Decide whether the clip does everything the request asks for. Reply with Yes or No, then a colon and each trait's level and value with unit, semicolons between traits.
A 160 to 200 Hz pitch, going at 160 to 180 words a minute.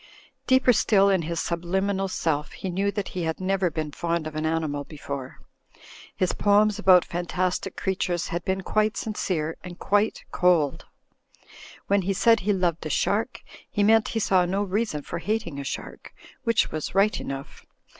Yes: medium, 185 Hz; average, 170 wpm